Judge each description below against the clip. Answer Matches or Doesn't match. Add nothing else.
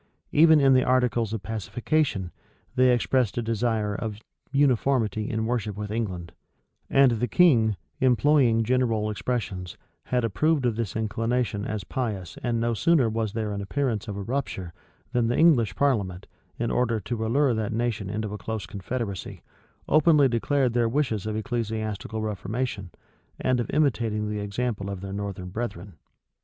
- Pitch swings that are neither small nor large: Matches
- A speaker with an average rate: Matches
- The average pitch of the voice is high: Doesn't match